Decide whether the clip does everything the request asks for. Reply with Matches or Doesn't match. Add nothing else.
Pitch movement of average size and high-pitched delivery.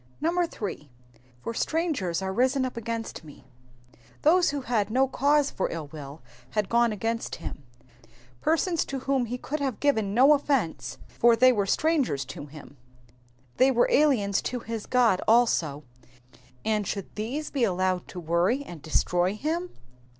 Doesn't match